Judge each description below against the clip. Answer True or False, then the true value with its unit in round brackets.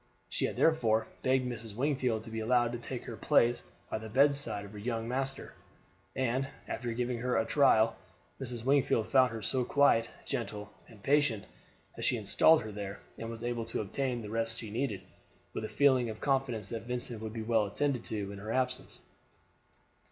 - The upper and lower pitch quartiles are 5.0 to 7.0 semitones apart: False (2.8 semitones)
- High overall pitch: False (115 Hz)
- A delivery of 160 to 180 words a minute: False (190 wpm)